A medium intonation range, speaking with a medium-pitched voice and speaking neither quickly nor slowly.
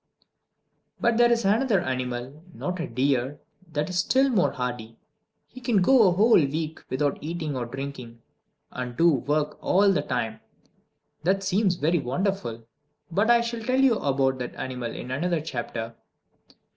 No: wide, 7.5 semitones; medium, 155 Hz; average, 160 wpm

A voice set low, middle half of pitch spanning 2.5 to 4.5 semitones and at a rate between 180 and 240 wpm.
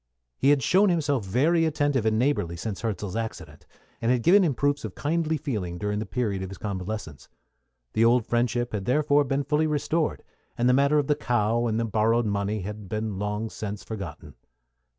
No: low, 115 Hz; wide, 5.5 semitones; average, 190 wpm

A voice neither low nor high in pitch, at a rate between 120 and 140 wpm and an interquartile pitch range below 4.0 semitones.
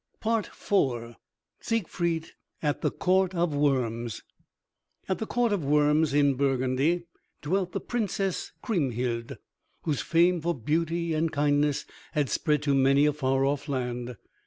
No: medium, 150 Hz; slow, 135 wpm; average, 4.3 semitones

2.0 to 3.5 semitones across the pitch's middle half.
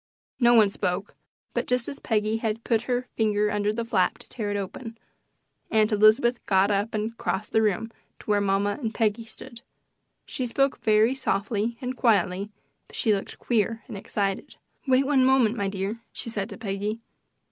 Yes: narrow, 2.5 semitones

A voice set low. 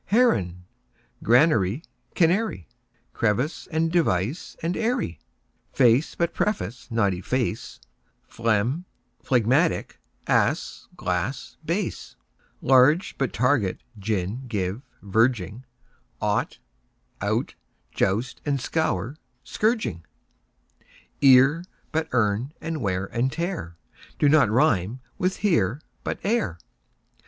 Yes: low, 125 Hz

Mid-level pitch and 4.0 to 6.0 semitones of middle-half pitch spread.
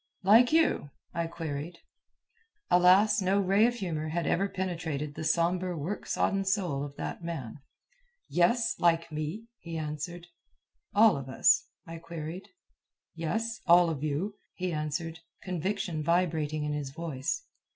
No: medium, 170 Hz; average, 3.6 semitones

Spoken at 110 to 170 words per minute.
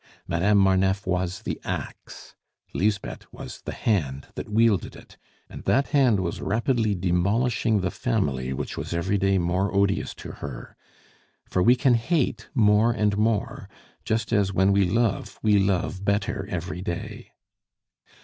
Yes: average, 150 wpm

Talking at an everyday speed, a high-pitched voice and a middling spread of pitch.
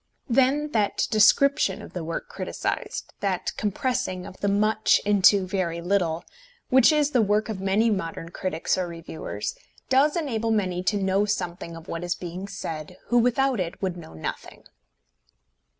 Yes: average, 160 wpm; high, 200 Hz; average, 4.4 semitones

